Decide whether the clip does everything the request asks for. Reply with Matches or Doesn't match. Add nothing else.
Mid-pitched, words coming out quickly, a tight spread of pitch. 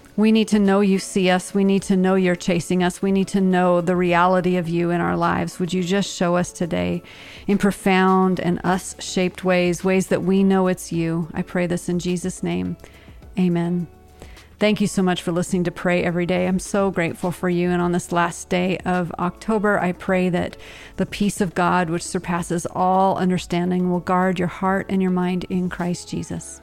Matches